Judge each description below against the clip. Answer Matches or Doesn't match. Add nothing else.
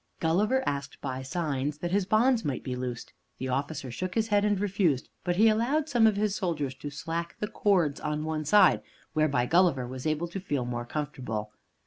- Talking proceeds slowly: Doesn't match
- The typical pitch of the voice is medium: Matches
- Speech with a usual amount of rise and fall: Doesn't match